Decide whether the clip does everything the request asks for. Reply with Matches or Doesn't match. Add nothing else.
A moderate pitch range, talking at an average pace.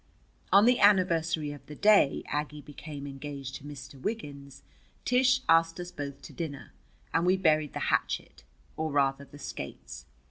Matches